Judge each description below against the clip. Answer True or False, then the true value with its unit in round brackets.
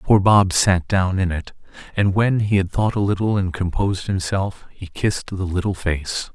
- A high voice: False (95 Hz)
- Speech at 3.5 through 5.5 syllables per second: True (4.7 syllables/s)